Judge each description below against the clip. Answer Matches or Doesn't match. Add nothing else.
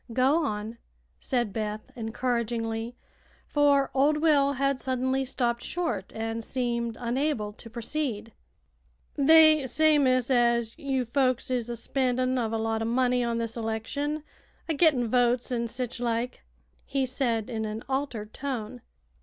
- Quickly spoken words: Doesn't match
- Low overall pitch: Doesn't match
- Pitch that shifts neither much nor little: Matches